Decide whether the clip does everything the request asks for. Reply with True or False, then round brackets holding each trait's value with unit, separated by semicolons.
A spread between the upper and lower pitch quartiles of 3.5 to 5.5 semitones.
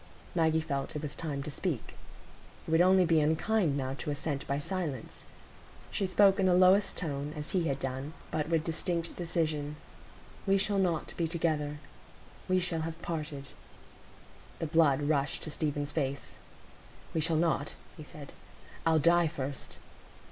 False (3.0 semitones)